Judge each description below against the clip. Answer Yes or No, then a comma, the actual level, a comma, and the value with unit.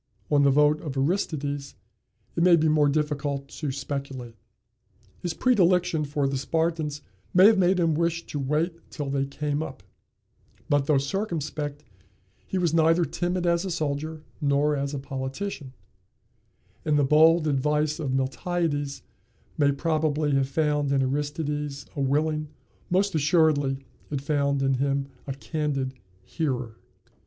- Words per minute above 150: No, average, 145 wpm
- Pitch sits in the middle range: Yes, medium, 150 Hz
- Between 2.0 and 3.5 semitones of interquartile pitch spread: Yes, narrow, 2.6 semitones